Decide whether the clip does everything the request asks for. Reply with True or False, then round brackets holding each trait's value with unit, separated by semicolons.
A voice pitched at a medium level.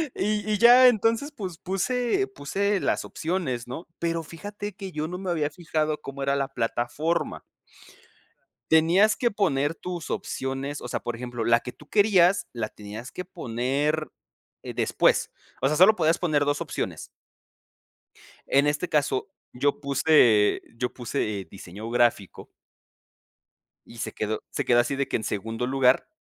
True (150 Hz)